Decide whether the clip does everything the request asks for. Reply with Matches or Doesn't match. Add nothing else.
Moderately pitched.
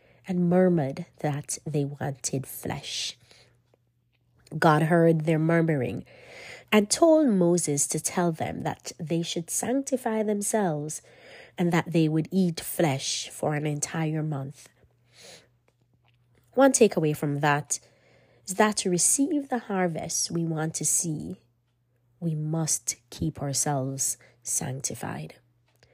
Matches